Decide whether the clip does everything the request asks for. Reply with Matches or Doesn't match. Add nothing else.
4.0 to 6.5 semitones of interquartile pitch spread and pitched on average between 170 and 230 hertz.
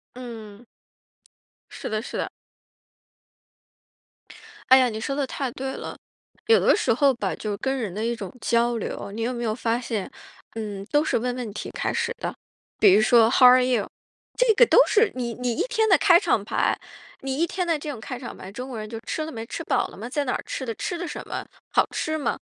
Doesn't match